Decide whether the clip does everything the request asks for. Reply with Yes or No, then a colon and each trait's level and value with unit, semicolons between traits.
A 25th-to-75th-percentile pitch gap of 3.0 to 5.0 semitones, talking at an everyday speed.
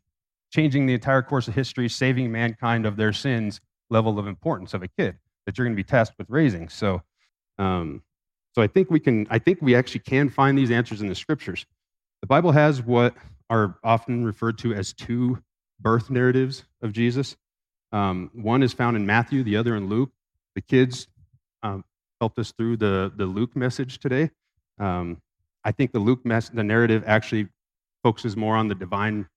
Yes: average, 3.7 semitones; average, 185 wpm